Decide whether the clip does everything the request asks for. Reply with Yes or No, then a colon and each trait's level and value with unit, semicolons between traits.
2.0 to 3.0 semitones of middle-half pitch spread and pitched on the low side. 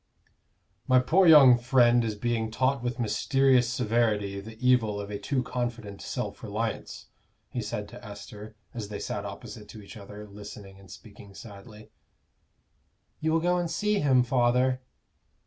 No: average, 3.6 semitones; low, 120 Hz